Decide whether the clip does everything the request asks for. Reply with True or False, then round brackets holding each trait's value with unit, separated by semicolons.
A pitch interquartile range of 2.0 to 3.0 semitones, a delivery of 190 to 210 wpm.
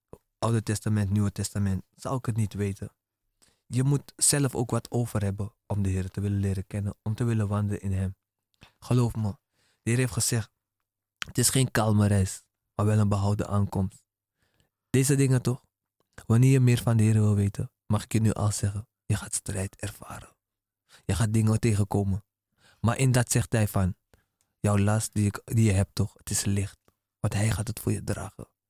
True (2.4 semitones; 195 wpm)